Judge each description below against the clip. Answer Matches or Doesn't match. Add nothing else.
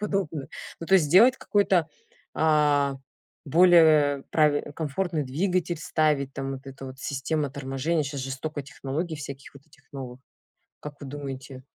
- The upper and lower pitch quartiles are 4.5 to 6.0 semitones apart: Doesn't match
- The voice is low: Doesn't match